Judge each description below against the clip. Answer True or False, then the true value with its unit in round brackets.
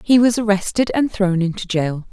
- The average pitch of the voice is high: True (205 Hz)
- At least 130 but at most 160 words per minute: False (200 wpm)